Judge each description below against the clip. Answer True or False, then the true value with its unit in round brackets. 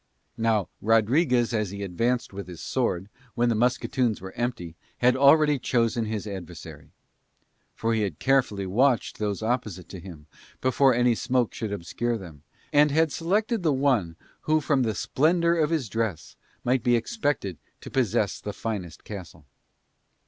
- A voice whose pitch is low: True (115 Hz)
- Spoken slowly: False (155 wpm)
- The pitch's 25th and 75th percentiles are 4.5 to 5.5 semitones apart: True (5.0 semitones)